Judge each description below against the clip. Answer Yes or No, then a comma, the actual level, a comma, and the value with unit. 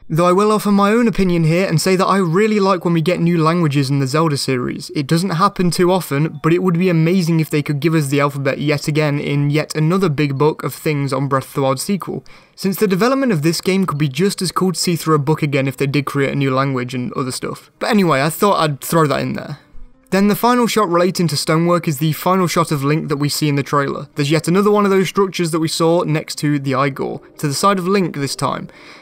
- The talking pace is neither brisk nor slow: No, fast, 270 wpm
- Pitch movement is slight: No, average, 4.3 semitones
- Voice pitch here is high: No, medium, 160 Hz